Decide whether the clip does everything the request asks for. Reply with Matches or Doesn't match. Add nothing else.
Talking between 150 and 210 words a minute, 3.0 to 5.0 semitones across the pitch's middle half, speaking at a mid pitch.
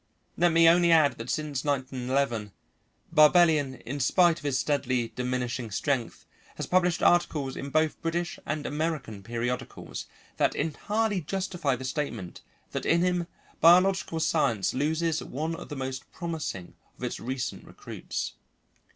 Doesn't match